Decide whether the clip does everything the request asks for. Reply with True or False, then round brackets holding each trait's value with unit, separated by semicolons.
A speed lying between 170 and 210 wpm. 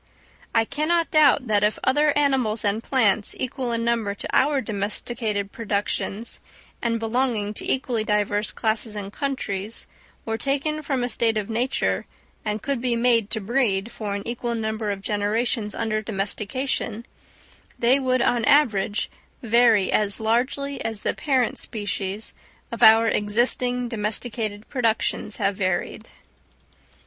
False (140 wpm)